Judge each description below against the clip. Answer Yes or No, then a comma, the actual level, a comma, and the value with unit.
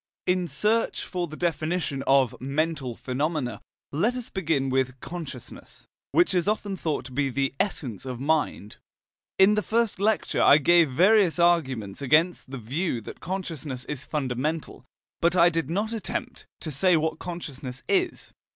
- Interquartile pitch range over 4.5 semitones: Yes, average, 5.2 semitones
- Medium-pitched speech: Yes, medium, 160 Hz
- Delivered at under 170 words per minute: Yes, average, 155 wpm